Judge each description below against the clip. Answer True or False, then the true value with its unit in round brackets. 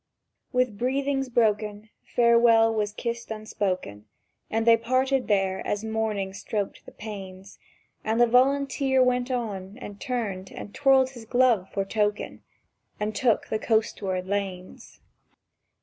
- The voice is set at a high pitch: True (220 Hz)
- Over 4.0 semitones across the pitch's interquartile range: False (3.6 semitones)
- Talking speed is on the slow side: True (130 wpm)